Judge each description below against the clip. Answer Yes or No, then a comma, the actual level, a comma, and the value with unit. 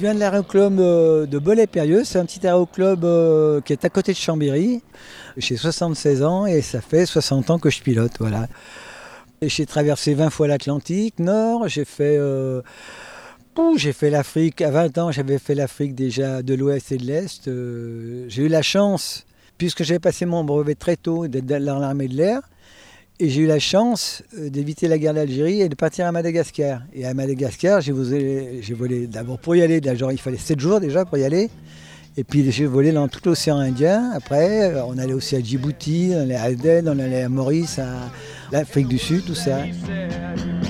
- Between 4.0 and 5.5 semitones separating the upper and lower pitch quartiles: Yes, average, 4.3 semitones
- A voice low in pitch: No, medium, 150 Hz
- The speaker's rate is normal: Yes, average, 195 wpm